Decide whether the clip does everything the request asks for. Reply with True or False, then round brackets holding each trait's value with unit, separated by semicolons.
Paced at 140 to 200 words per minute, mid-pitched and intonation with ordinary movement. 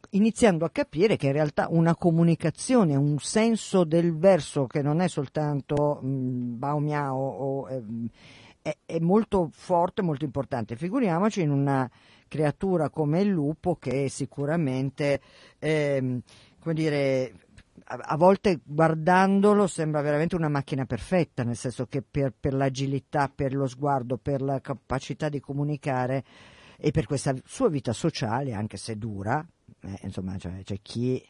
True (145 wpm; 145 Hz; 3.8 semitones)